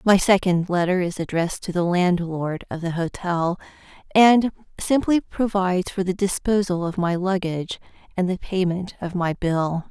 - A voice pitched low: No, medium, 185 Hz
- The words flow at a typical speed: Yes, average, 155 wpm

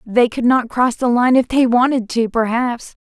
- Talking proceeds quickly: Yes, fast, 210 wpm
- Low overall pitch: No, high, 240 Hz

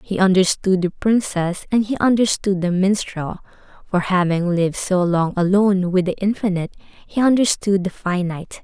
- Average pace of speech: Yes, average, 155 wpm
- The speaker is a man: No, female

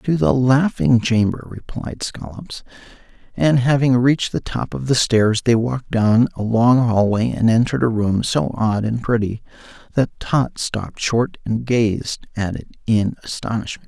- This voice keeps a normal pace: Yes, average, 165 wpm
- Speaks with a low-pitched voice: Yes, low, 115 Hz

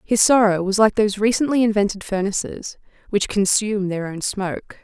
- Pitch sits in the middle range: No, high, 205 Hz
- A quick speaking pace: No, average, 160 wpm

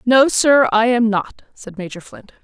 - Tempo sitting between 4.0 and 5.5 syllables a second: Yes, 4.3 syllables/s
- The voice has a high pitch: Yes, high, 230 Hz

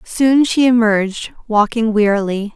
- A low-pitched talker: No, high, 225 Hz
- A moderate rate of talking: No, slow, 120 wpm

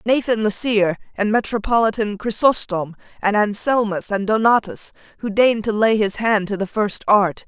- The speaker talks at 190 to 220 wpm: No, average, 160 wpm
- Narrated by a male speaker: No, female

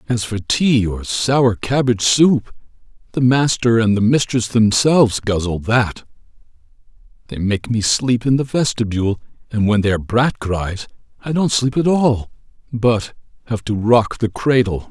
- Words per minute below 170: Yes, average, 155 wpm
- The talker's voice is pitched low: Yes, low, 115 Hz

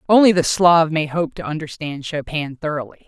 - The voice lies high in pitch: No, medium, 160 Hz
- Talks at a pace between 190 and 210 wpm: No, average, 175 wpm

